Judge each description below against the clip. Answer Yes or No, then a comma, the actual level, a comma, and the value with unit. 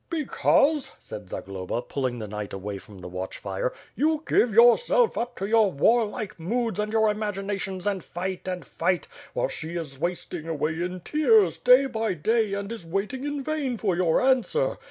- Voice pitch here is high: Yes, high, 200 Hz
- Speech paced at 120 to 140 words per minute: No, average, 175 wpm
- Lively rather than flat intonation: Yes, wide, 6.9 semitones